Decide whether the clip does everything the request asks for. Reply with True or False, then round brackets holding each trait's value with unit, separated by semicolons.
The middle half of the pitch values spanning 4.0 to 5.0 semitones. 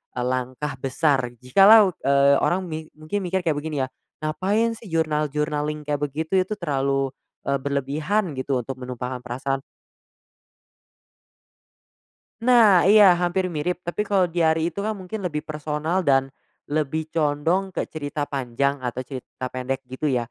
True (4.5 semitones)